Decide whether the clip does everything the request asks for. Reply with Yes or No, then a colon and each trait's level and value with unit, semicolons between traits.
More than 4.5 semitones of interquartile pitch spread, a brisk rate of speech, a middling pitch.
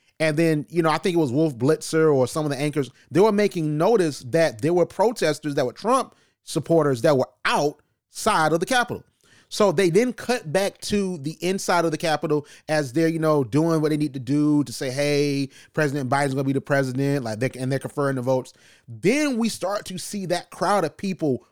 No: average, 3.7 semitones; fast, 225 wpm; medium, 155 Hz